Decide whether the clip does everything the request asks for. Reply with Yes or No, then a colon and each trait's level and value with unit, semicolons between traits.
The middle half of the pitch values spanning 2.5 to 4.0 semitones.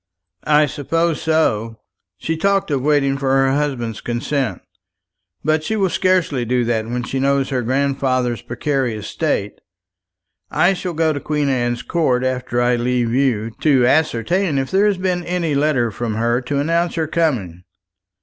No: average, 4.6 semitones